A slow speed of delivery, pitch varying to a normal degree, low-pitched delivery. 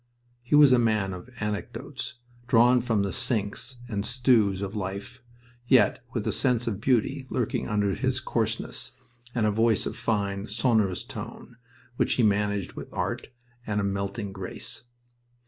No: average, 160 wpm; average, 3.5 semitones; low, 110 Hz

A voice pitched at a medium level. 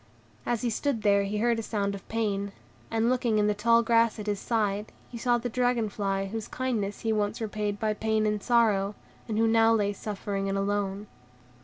No: high, 215 Hz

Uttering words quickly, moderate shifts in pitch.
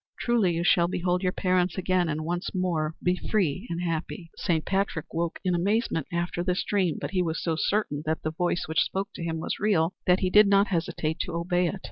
No: fast, 220 wpm; narrow, 2.3 semitones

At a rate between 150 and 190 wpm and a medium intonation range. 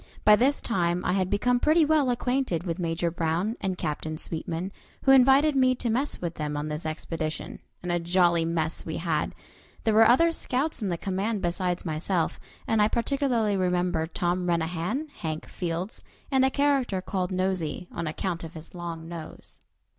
No: average, 175 wpm; wide, 6.1 semitones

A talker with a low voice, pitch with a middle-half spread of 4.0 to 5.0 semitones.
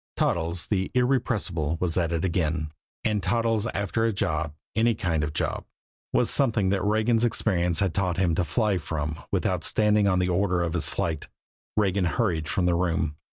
Yes: very low, 90 Hz; average, 4.4 semitones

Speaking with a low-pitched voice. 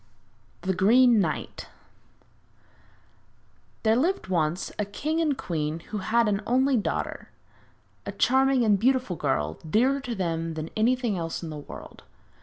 No: high, 210 Hz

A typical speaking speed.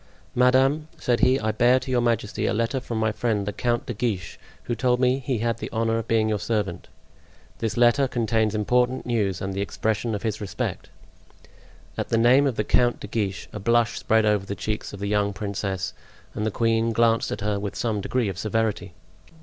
No: fast, 210 wpm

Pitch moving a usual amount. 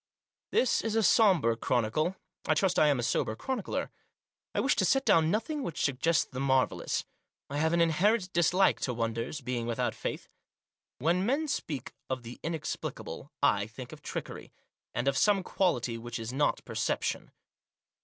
No: wide, 7.5 semitones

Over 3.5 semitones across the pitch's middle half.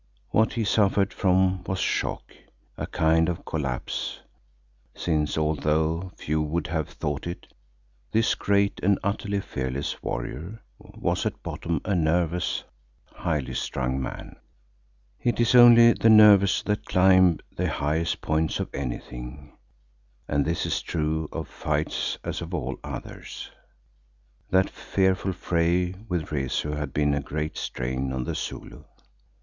Yes: average, 4.2 semitones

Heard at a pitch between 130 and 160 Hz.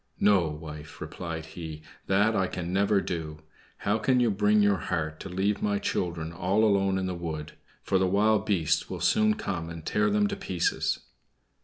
No: very low, 95 Hz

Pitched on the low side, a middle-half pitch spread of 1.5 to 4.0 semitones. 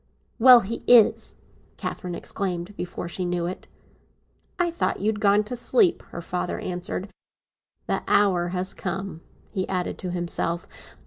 No: medium, 185 Hz; average, 3.0 semitones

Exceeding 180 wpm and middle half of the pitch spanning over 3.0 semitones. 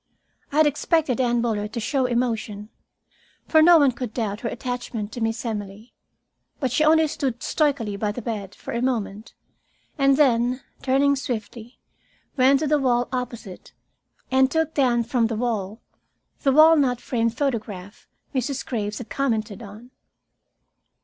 No: average, 150 wpm; average, 3.6 semitones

